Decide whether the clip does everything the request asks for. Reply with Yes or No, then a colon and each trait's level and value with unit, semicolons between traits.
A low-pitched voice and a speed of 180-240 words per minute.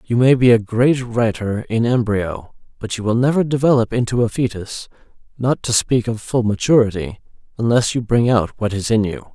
Yes: low, 115 Hz; average, 195 wpm